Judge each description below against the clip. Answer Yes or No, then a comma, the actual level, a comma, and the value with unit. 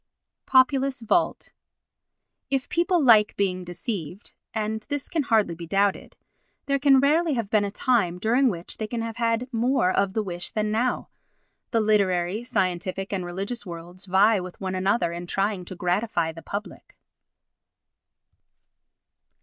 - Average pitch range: Yes, average, 4.8 semitones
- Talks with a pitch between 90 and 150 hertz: No, high, 210 Hz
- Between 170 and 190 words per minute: No, average, 140 wpm